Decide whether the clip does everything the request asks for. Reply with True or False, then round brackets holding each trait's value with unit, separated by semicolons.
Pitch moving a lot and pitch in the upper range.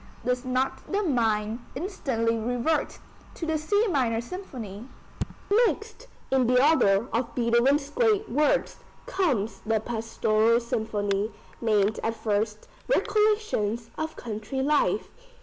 True (5.7 semitones; 240 Hz)